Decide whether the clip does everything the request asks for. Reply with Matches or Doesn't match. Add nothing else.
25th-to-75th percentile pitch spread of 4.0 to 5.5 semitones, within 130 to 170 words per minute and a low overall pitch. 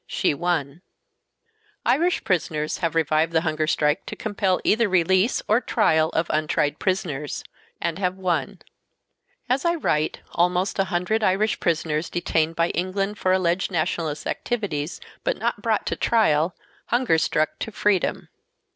Doesn't match